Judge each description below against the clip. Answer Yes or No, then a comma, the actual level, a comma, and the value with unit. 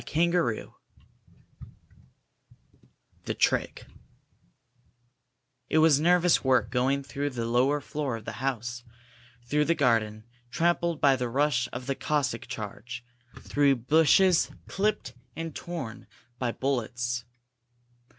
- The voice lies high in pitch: No, low, 135 Hz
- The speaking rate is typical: No, slow, 110 wpm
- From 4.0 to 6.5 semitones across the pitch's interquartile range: Yes, average, 4.5 semitones